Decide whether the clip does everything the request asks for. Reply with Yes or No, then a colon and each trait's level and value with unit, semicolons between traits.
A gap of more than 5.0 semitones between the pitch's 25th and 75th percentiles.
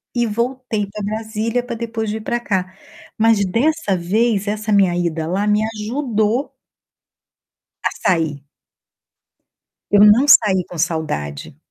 No: average, 3.7 semitones